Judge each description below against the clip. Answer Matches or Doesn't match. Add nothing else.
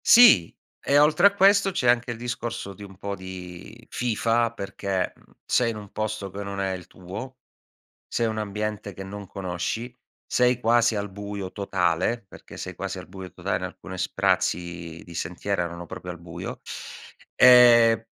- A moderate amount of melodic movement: Matches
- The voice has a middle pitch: Doesn't match